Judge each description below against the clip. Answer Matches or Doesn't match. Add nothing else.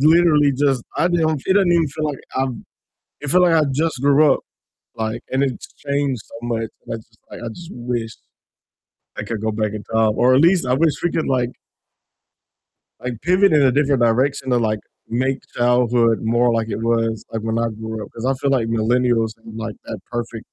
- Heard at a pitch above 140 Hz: Doesn't match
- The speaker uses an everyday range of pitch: Matches